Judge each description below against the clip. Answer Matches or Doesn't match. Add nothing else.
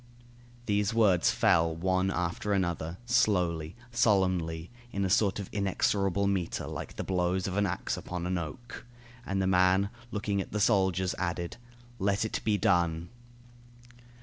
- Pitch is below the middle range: Matches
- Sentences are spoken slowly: Doesn't match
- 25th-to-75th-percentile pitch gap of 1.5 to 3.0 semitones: Matches